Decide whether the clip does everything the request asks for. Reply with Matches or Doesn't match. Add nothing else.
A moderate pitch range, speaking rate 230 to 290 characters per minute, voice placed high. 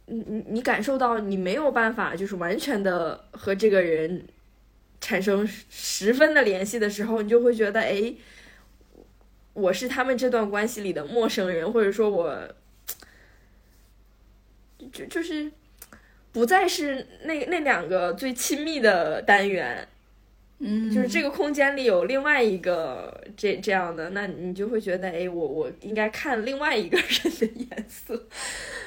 Doesn't match